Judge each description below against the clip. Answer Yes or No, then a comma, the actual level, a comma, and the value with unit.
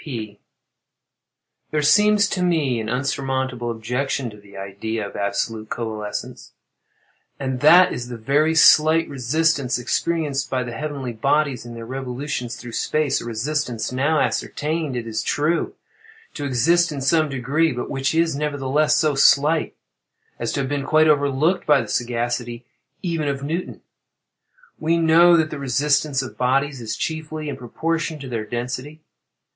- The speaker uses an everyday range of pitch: Yes, average, 4.3 semitones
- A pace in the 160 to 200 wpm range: No, average, 150 wpm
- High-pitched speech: No, medium, 140 Hz